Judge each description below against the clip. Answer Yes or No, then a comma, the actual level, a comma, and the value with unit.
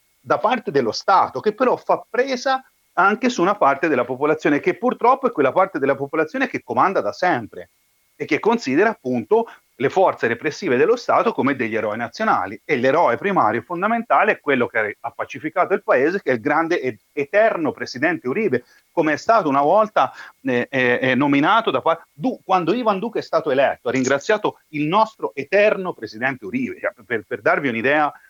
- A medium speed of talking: No, fast, 180 wpm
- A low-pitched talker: No, medium, 185 Hz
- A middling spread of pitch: No, wide, 8.6 semitones